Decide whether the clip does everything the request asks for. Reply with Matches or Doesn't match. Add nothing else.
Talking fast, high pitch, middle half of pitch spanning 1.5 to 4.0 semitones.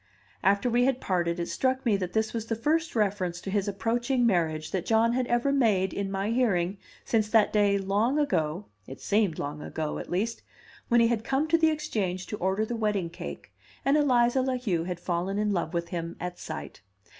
Doesn't match